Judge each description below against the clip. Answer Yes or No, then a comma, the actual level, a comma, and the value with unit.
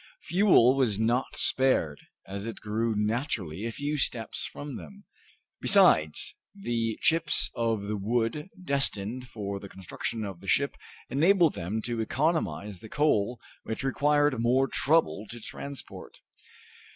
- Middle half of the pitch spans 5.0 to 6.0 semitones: Yes, average, 5.3 semitones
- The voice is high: No, low, 115 Hz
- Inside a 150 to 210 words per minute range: No, slow, 135 wpm